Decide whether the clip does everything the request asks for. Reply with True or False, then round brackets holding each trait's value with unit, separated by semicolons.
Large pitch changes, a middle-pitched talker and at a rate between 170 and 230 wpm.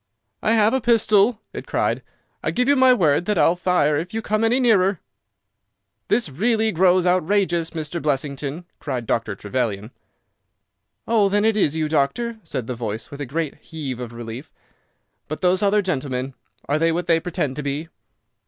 True (6.8 semitones; 165 Hz; 175 wpm)